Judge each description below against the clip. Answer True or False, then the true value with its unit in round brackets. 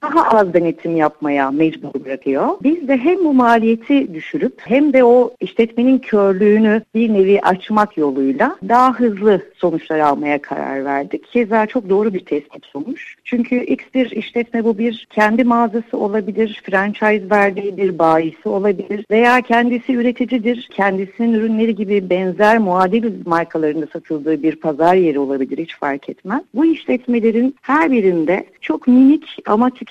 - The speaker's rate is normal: False (145 wpm)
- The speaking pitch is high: True (215 Hz)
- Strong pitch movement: True (6.2 semitones)